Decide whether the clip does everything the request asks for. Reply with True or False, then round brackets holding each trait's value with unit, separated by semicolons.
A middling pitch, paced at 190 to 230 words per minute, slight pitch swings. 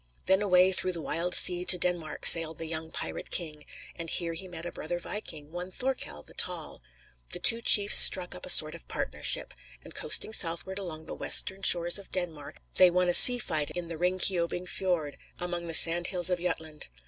True (175 Hz; 200 wpm; 2.0 semitones)